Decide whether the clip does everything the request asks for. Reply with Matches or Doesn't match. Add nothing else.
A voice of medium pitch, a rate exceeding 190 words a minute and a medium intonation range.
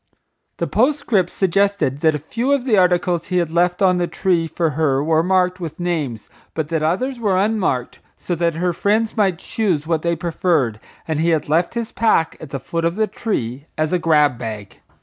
Matches